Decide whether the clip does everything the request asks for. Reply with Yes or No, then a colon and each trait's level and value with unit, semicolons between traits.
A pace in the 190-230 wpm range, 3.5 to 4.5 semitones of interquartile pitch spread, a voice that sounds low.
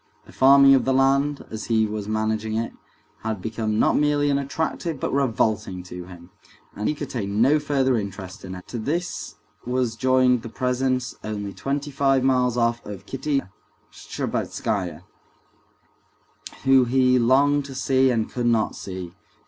No: average, 160 wpm; average, 3.9 semitones; low, 125 Hz